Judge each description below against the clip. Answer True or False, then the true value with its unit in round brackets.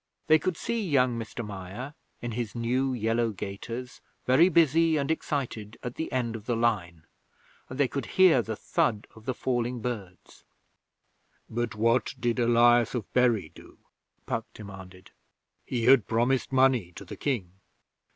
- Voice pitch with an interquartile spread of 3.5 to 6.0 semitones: False (3.1 semitones)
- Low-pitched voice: True (120 Hz)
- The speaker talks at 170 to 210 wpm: False (155 wpm)